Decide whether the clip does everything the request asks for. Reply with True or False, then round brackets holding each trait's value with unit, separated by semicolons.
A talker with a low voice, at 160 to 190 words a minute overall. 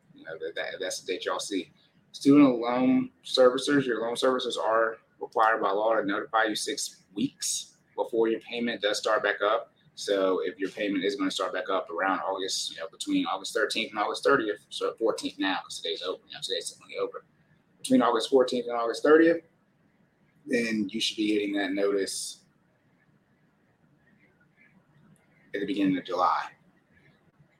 False (145 Hz; 170 wpm)